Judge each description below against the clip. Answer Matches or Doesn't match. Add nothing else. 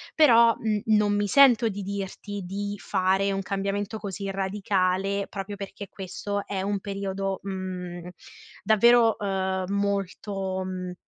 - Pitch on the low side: Doesn't match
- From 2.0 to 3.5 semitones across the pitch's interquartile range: Doesn't match